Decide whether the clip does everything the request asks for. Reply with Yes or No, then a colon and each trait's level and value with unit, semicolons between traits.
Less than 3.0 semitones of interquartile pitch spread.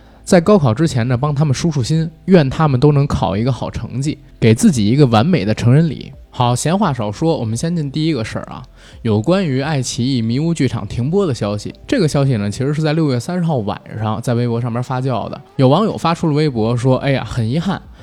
No: wide, 5.4 semitones